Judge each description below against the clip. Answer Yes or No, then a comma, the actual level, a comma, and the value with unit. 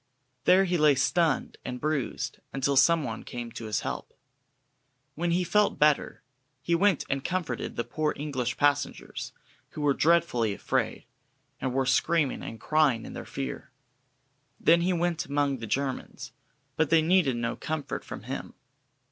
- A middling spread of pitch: Yes, average, 4.4 semitones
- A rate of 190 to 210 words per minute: No, average, 155 wpm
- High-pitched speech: No, medium, 145 Hz